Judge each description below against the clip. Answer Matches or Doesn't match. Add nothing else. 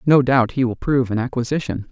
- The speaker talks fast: Matches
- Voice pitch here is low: Matches